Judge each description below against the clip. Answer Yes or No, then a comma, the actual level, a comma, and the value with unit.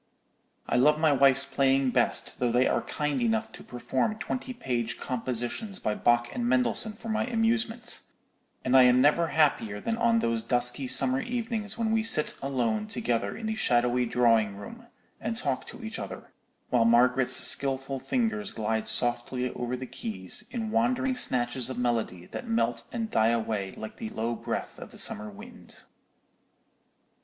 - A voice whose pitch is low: Yes, low, 130 Hz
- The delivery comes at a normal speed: Yes, average, 165 wpm